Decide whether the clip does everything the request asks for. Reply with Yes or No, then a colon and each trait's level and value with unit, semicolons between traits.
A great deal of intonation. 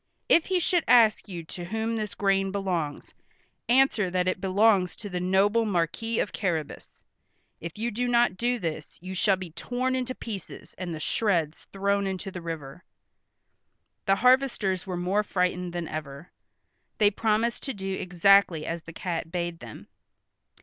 No: average, 4.2 semitones